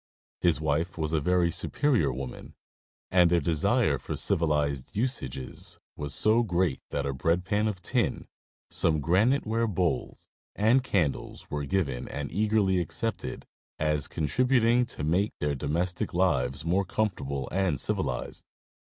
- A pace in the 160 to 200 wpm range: No, average, 140 wpm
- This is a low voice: Yes, very low, 85 Hz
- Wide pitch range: Yes, wide, 6.0 semitones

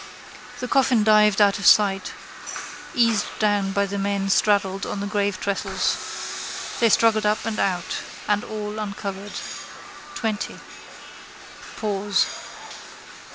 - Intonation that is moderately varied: No, narrow, 1.3 semitones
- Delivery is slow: Yes, slow, 110 wpm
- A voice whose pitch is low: No, high, 205 Hz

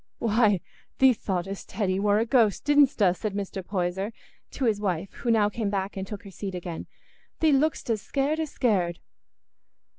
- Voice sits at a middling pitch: No, high, 205 Hz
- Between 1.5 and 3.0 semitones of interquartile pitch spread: No, average, 3.6 semitones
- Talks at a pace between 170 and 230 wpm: Yes, average, 175 wpm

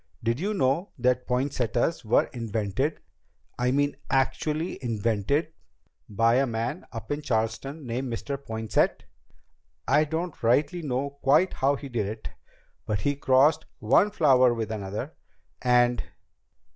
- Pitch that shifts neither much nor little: Yes, average, 4.0 semitones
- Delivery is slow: Yes, slow, 130 wpm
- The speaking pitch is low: Yes, low, 130 Hz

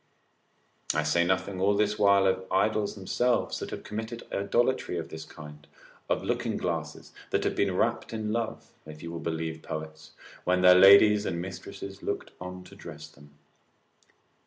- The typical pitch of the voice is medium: No, very low, 95 Hz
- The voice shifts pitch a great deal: No, average, 4.0 semitones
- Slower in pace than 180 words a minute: Yes, average, 165 wpm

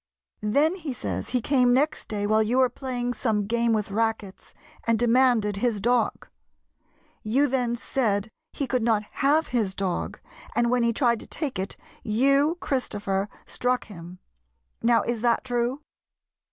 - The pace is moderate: Yes, average, 155 wpm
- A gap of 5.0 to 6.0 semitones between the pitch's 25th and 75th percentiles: No, average, 3.3 semitones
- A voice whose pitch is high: Yes, high, 235 Hz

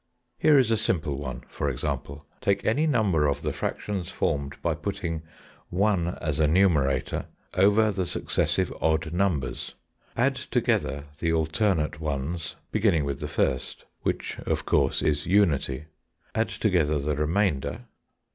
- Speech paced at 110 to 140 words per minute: Yes, slow, 135 wpm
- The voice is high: No, very low, 80 Hz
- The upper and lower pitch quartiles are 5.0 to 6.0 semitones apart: Yes, average, 5.3 semitones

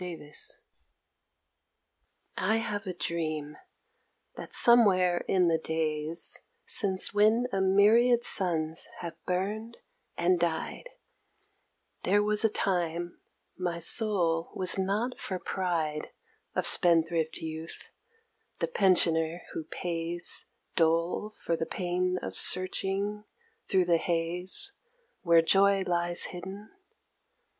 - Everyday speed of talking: No, slow, 105 wpm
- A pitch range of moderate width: Yes, average, 3.2 semitones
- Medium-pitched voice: Yes, medium, 180 Hz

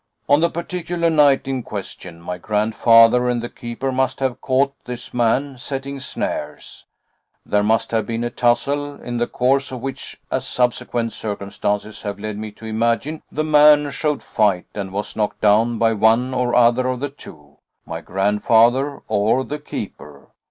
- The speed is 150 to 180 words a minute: Yes, average, 165 wpm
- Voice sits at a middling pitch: No, low, 120 Hz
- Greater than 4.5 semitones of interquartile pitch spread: No, average, 4.0 semitones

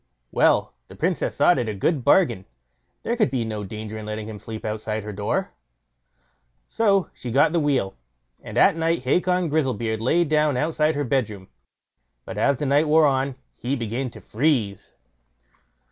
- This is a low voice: Yes, low, 130 Hz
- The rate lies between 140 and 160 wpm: No, average, 170 wpm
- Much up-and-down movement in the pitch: Yes, wide, 6.0 semitones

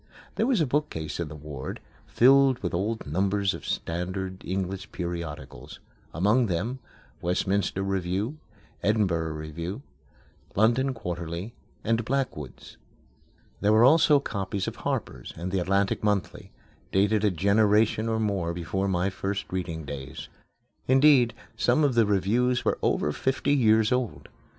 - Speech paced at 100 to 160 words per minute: Yes, slow, 135 wpm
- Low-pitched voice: Yes, low, 100 Hz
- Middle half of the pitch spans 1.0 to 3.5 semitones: No, average, 4.8 semitones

